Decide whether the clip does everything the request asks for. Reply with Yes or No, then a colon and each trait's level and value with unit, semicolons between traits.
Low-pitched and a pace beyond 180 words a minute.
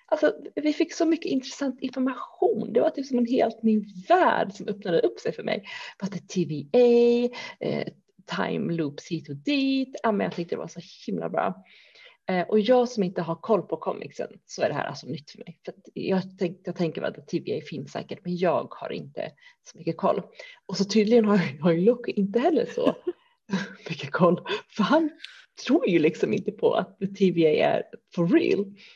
No: high, 220 Hz; fast, 195 wpm